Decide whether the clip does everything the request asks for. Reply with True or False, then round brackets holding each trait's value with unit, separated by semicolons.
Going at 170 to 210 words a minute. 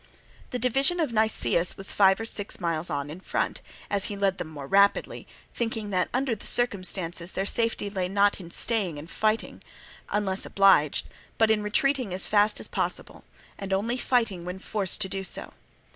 True (180 wpm)